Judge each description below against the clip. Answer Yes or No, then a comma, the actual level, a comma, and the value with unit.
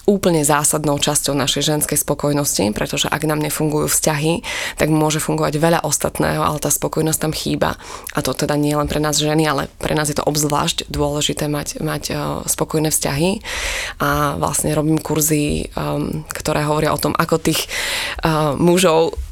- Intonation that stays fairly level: Yes, narrow, 1.3 semitones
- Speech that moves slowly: No, average, 160 wpm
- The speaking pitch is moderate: Yes, medium, 150 Hz